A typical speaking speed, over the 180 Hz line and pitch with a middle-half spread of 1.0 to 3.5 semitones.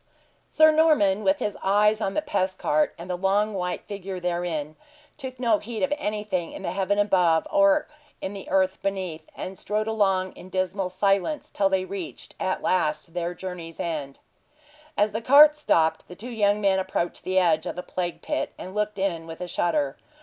Yes: average, 190 wpm; high, 190 Hz; average, 2.9 semitones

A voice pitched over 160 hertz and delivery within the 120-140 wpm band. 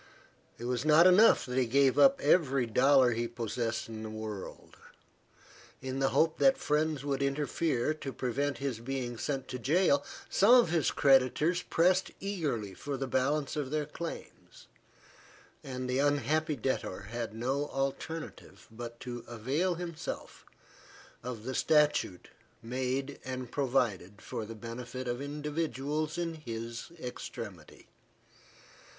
No: low, 135 Hz; slow, 135 wpm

